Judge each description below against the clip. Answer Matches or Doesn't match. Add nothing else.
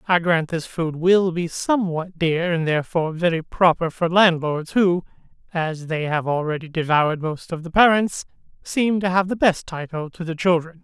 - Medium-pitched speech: Matches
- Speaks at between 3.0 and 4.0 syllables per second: Doesn't match